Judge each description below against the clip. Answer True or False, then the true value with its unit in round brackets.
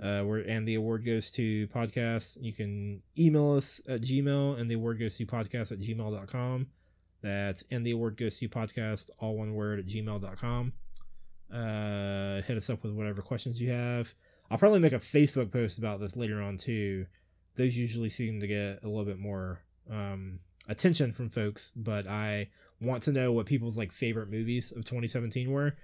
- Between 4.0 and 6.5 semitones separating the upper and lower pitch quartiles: False (3.0 semitones)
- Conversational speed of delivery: True (185 wpm)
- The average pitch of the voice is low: True (110 Hz)